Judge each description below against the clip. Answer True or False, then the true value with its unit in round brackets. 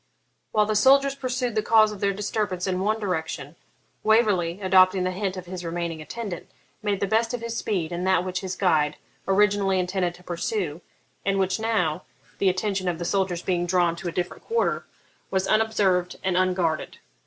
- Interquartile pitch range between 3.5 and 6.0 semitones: False (3.0 semitones)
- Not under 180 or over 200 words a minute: True (185 wpm)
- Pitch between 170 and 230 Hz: True (190 Hz)